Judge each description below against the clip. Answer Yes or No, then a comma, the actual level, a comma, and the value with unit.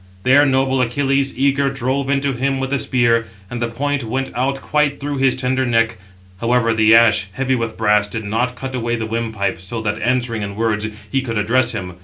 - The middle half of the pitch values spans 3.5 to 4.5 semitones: No, average, 3.0 semitones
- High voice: No, low, 125 Hz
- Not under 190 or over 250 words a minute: Yes, fast, 205 wpm